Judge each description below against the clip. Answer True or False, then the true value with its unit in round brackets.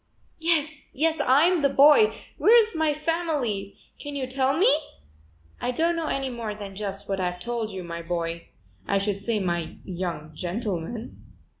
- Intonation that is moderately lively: False (8.0 semitones)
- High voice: True (235 Hz)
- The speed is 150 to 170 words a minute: True (160 wpm)